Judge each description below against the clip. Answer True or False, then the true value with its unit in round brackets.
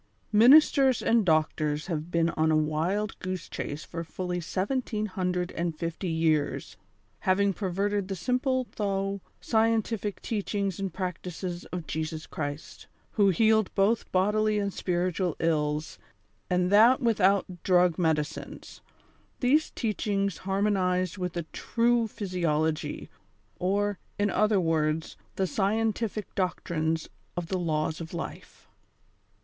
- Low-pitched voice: False (185 Hz)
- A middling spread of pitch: True (3.9 semitones)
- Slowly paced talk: True (125 wpm)